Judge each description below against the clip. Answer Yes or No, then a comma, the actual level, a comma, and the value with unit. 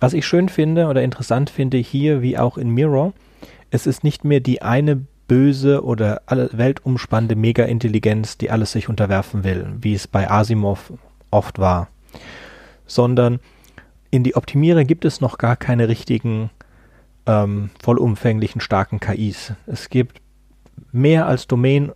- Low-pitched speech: Yes, low, 120 Hz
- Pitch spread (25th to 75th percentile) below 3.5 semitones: No, average, 3.8 semitones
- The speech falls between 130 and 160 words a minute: Yes, average, 140 wpm